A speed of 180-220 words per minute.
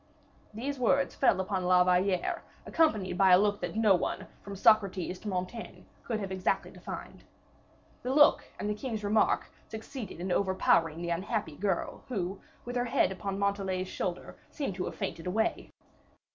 No: average, 165 wpm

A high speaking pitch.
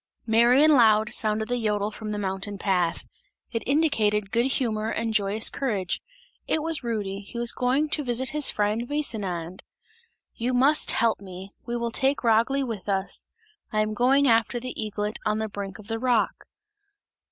Yes: high, 225 Hz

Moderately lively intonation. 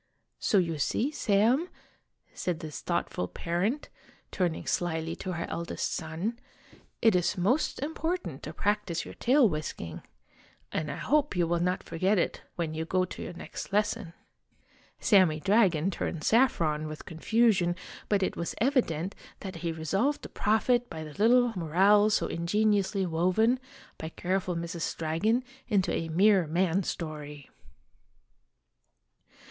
Yes: average, 4.7 semitones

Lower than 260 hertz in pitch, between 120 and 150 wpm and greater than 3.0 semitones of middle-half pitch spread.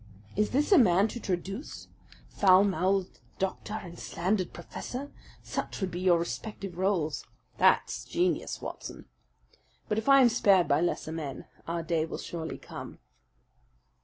Yes: high, 190 Hz; average, 145 wpm; average, 3.8 semitones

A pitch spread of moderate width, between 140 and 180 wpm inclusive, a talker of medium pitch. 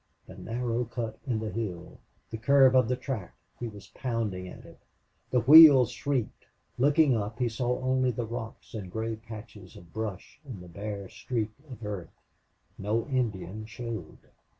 No: average, 3.2 semitones; average, 165 wpm; low, 115 Hz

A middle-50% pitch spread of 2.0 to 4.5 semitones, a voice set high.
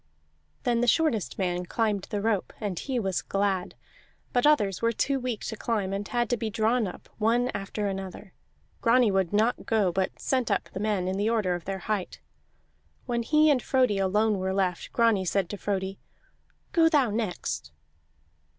Yes: average, 3.5 semitones; high, 210 Hz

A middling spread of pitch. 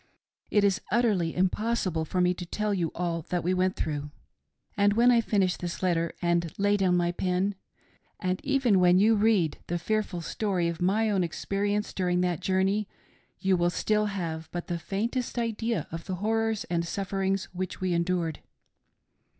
Yes: average, 3.1 semitones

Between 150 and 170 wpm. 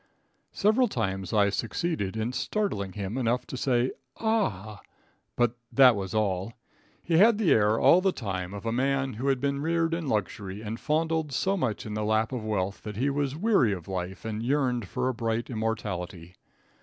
No: average, 185 wpm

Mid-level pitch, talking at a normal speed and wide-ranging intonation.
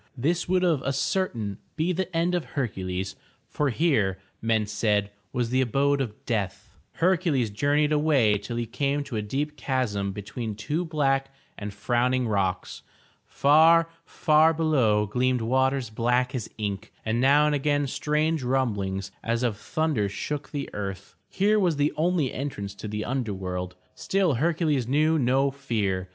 No: low, 130 Hz; average, 160 wpm; wide, 6.0 semitones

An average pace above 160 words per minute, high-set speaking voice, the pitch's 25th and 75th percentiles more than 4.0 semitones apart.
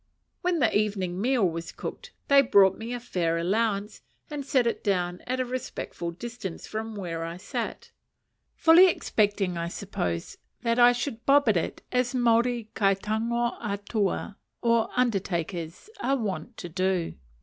No: average, 155 wpm; high, 215 Hz; average, 4.8 semitones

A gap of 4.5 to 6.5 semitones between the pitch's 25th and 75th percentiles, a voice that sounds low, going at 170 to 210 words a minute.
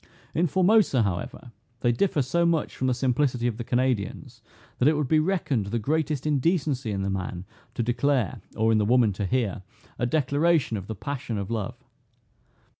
Yes: average, 5.1 semitones; low, 125 Hz; average, 185 wpm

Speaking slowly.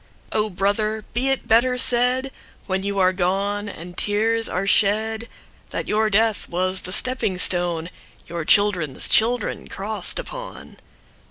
Yes: slow, 120 wpm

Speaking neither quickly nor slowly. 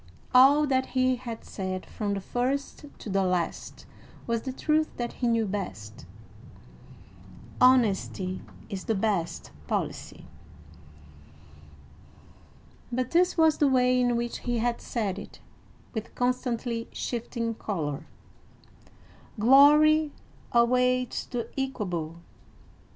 No: slow, 110 wpm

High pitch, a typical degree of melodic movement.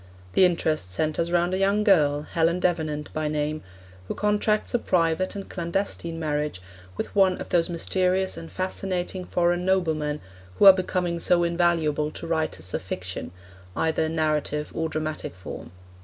No: medium, 170 Hz; average, 3.1 semitones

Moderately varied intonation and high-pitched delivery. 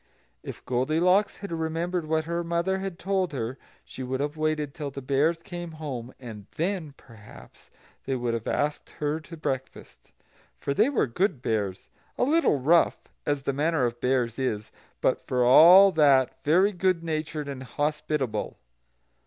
No: average, 4.6 semitones; medium, 150 Hz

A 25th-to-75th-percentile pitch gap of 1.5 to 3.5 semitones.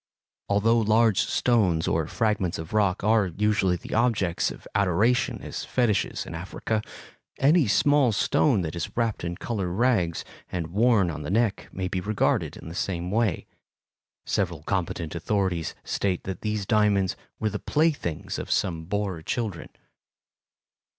No: average, 4.1 semitones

